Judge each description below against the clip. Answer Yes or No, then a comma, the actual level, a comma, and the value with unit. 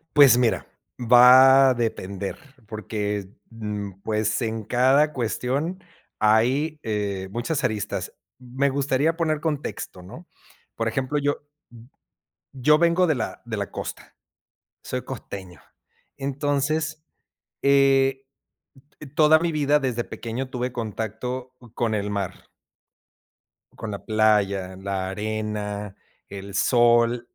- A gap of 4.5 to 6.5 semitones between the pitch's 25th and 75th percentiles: Yes, average, 4.8 semitones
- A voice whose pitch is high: No, low, 120 Hz